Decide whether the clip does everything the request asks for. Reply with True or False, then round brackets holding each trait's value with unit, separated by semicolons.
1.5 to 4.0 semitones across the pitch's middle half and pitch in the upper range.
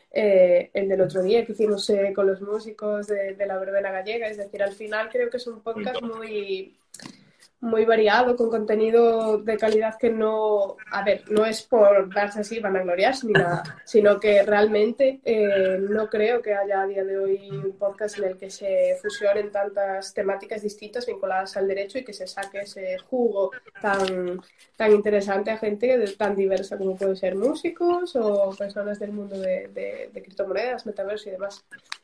True (2.4 semitones; 210 Hz)